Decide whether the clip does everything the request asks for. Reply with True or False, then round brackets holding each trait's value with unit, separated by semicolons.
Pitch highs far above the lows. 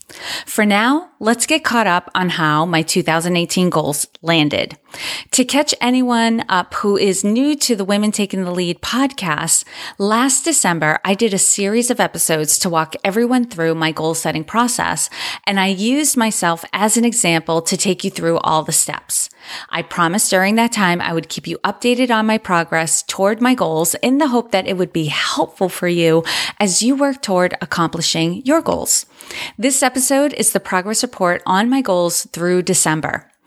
True (5.7 semitones)